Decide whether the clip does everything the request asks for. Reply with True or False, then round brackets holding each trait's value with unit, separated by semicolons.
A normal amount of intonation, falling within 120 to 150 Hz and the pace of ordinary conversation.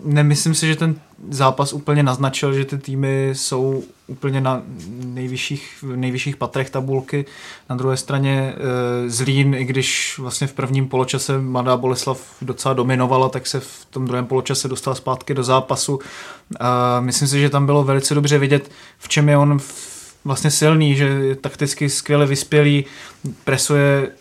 False (1.6 semitones; 135 Hz; 155 wpm)